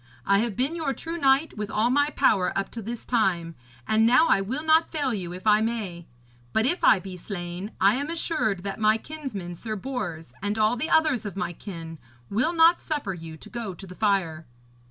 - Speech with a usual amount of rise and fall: No, wide, 6.1 semitones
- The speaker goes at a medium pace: No, fast, 215 wpm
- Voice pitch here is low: No, high, 215 Hz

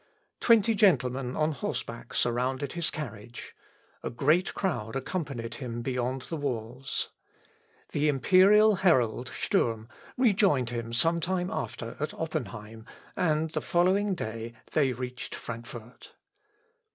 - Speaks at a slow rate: Yes, slow, 115 wpm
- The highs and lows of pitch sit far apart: Yes, wide, 6.3 semitones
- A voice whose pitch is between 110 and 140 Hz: Yes, low, 135 Hz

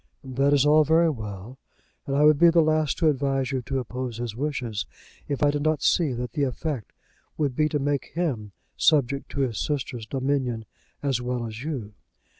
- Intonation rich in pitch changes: No, average, 3.3 semitones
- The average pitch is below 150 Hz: Yes, low, 135 Hz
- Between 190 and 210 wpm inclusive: Yes, average, 195 wpm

